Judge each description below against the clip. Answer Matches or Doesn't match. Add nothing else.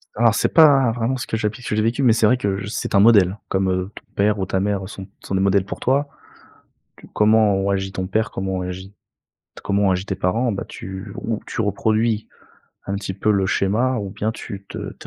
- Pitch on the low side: Matches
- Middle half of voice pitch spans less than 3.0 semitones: Matches